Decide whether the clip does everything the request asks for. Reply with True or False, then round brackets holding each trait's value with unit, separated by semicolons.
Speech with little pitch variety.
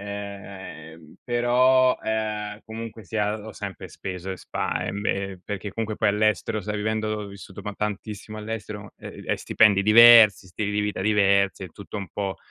True (1.7 semitones)